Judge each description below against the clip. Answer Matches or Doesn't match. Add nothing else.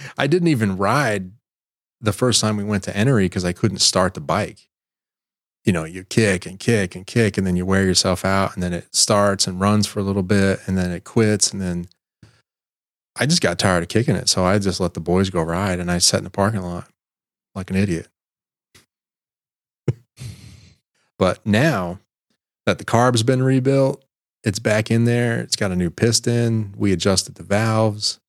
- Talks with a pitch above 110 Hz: Doesn't match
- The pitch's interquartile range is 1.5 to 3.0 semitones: Doesn't match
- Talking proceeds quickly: Doesn't match